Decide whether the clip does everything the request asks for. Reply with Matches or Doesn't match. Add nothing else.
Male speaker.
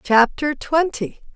Doesn't match